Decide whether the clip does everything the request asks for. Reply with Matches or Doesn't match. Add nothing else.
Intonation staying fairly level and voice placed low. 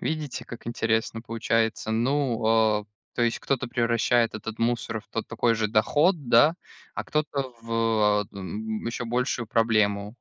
Matches